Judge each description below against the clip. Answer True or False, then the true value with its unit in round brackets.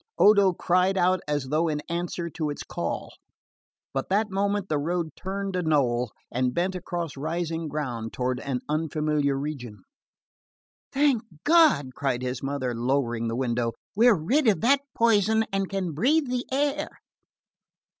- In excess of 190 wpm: False (150 wpm)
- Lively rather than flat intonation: True (6.5 semitones)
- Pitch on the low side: False (165 Hz)